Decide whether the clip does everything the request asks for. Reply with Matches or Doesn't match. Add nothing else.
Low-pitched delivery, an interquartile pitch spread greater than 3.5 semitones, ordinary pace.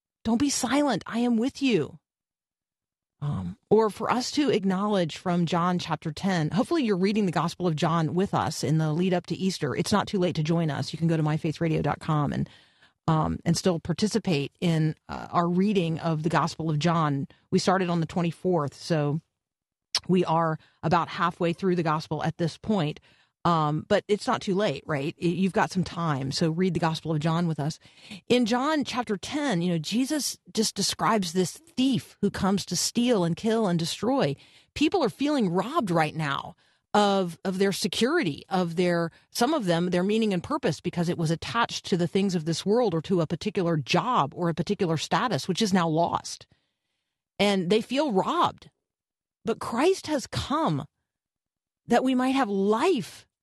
Doesn't match